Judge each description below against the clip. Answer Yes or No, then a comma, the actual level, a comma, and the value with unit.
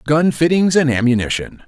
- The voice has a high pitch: No, medium, 140 Hz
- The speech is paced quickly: No, average, 145 wpm